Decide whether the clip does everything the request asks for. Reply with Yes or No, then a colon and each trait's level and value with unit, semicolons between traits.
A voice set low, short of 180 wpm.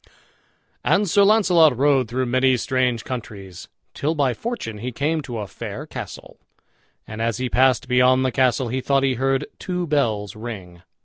Yes: low, 130 Hz; average, 170 wpm